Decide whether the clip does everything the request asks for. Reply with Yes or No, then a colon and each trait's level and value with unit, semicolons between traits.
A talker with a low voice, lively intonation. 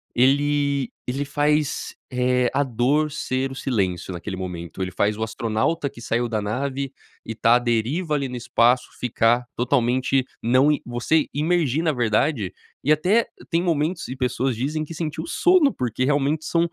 No: low, 130 Hz; average, 4.1 semitones